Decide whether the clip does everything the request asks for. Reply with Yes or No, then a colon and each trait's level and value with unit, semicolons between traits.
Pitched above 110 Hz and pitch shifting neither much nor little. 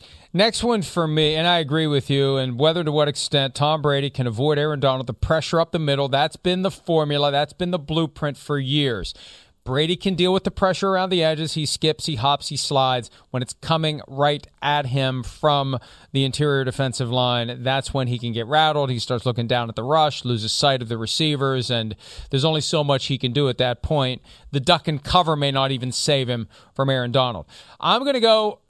Yes: medium, 140 Hz; average, 3.6 semitones